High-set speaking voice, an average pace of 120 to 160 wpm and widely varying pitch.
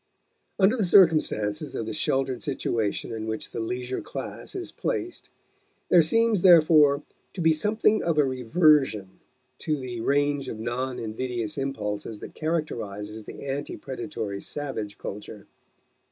No: low, 135 Hz; average, 140 wpm; wide, 6.1 semitones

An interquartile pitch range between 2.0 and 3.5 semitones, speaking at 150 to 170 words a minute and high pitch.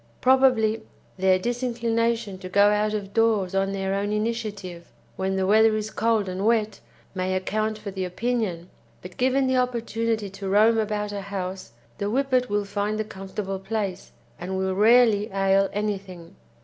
Yes: average, 2.8 semitones; average, 160 wpm; high, 205 Hz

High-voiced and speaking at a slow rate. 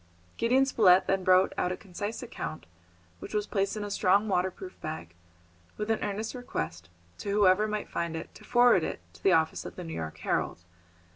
No: high, 195 Hz; average, 195 wpm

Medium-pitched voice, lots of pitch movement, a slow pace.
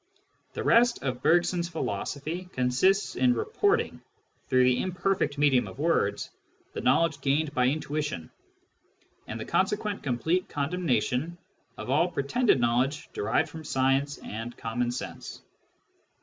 Yes: medium, 145 Hz; wide, 5.9 semitones; slow, 130 wpm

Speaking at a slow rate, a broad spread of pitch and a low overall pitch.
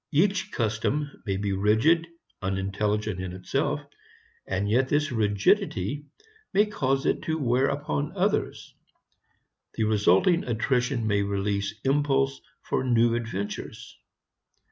Yes: slow, 115 wpm; wide, 5.9 semitones; low, 120 Hz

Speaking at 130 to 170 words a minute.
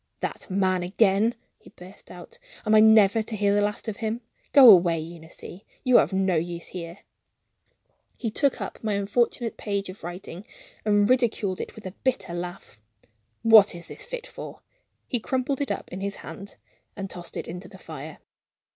No: average, 180 wpm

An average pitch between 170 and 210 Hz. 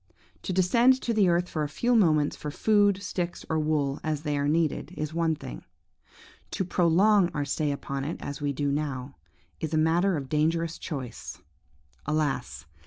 No: medium, 155 Hz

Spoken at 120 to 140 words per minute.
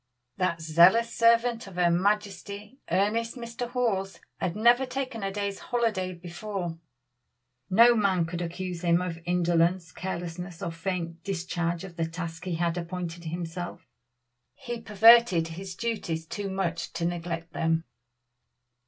Yes: slow, 135 wpm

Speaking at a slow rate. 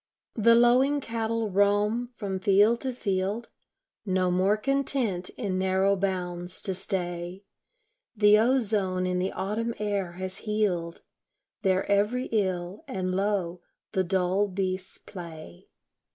Yes: slow, 125 wpm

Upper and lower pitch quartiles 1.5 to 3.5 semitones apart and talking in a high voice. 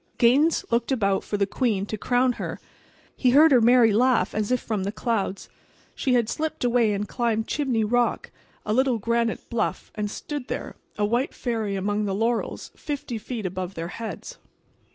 Yes: average, 3.2 semitones; high, 230 Hz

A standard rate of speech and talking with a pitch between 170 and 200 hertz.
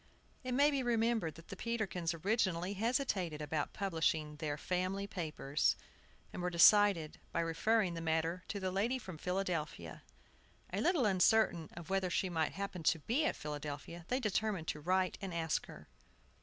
Yes: average, 165 wpm; medium, 185 Hz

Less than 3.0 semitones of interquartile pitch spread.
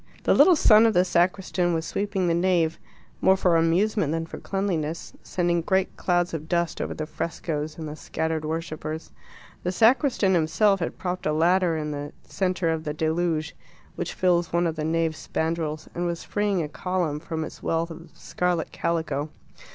Yes: narrow, 2.4 semitones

